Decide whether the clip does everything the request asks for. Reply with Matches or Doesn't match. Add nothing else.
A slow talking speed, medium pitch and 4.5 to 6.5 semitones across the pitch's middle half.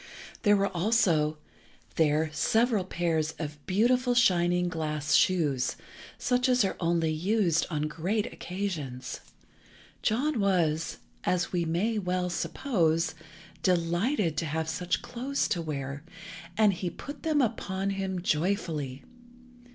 Matches